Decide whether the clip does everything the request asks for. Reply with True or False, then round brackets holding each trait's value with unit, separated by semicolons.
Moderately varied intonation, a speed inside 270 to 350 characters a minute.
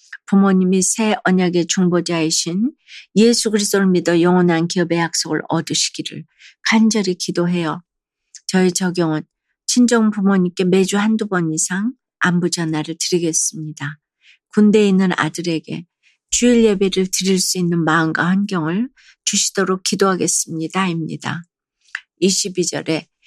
True (3.0 semitones; 290 characters per minute)